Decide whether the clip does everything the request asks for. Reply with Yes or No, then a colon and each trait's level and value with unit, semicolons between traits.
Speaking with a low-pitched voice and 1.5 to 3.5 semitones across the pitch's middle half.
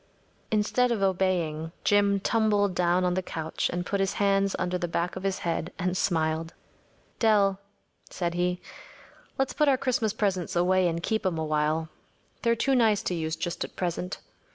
No: medium, 185 Hz; average, 3.0 semitones